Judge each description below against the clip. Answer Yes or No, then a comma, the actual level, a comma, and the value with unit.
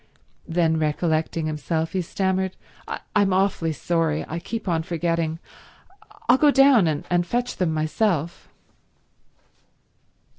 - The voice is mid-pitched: Yes, medium, 170 Hz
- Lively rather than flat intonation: No, average, 3.2 semitones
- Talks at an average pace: No, slow, 100 wpm